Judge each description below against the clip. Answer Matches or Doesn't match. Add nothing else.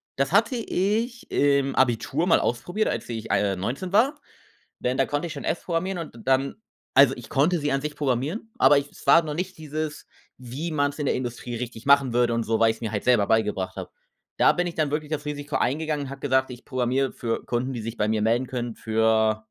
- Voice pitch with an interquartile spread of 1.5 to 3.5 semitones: Doesn't match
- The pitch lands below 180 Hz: Matches